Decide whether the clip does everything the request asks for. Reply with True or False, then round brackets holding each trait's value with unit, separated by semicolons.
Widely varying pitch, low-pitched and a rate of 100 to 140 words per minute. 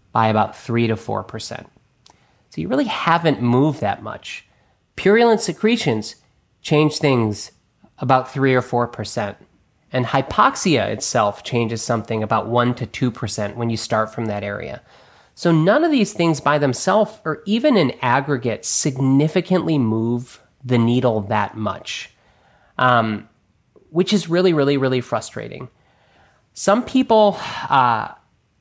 True (6.4 semitones; 130 Hz; 135 wpm)